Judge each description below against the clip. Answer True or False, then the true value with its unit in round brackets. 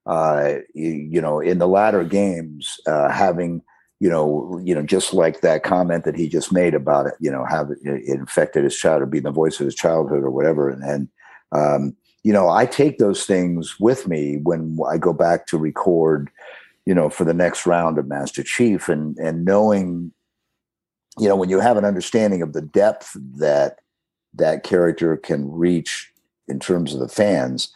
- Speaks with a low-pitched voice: True (80 Hz)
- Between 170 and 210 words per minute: True (195 wpm)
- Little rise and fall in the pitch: False (3.3 semitones)